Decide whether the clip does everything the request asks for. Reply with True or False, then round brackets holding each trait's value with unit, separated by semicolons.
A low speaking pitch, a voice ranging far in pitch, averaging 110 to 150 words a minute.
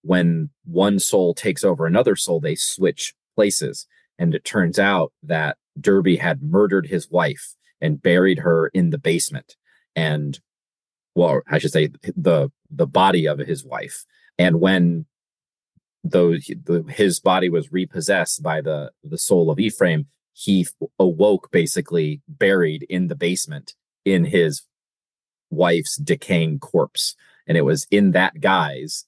True (90 Hz; 7.2 semitones; 140 wpm)